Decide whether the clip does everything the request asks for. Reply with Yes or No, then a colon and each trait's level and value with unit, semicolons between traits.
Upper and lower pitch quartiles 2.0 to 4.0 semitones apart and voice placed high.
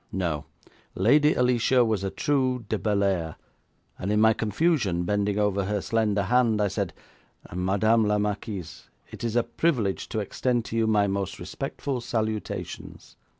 No: average, 3.0 semitones; low, 105 Hz